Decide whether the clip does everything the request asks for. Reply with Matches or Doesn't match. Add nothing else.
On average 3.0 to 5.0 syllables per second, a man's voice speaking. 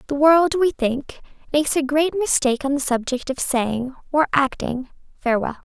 Doesn't match